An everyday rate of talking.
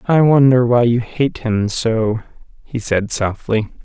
Yes: average, 155 wpm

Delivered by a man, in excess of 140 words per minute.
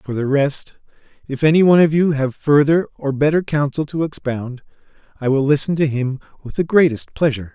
Yes: male; average, 190 wpm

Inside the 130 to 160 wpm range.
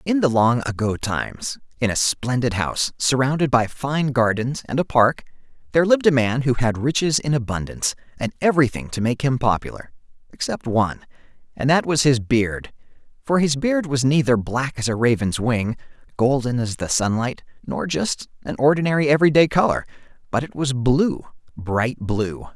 No: average, 175 wpm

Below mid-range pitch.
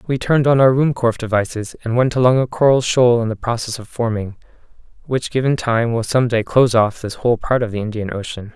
Yes: low, 120 Hz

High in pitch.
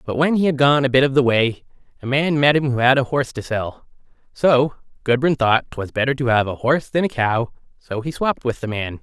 No: low, 130 Hz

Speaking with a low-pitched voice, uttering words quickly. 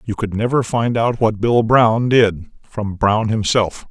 No: low, 110 Hz; average, 185 wpm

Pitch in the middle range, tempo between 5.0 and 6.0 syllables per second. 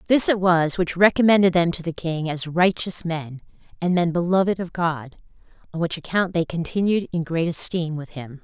Yes: medium, 170 Hz; 5.1 syllables/s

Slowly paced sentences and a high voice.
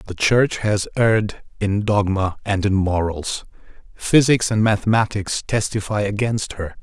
No: slow, 130 wpm; low, 105 Hz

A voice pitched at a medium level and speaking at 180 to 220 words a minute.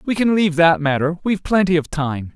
Yes: medium, 170 Hz; fast, 205 wpm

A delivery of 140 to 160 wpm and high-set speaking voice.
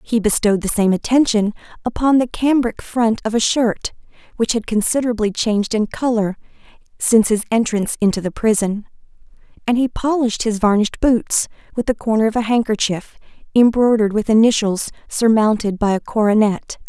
Yes: average, 155 wpm; high, 220 Hz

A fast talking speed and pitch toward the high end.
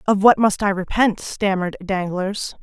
No: average, 160 wpm; high, 195 Hz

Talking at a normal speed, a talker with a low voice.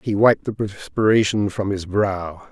Yes: average, 165 wpm; low, 100 Hz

